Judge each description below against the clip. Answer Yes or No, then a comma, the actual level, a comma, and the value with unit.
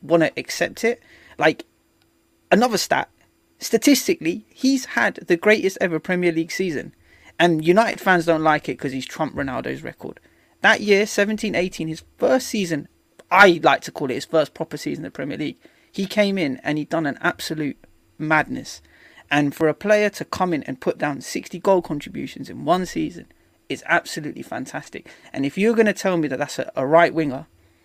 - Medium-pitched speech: Yes, medium, 180 Hz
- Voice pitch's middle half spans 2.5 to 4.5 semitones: No, wide, 5.4 semitones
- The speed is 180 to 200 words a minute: Yes, average, 185 wpm